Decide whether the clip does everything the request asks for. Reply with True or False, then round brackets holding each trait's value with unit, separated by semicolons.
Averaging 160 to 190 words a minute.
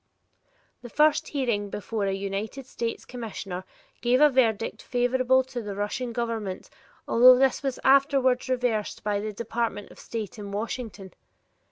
False (145 wpm)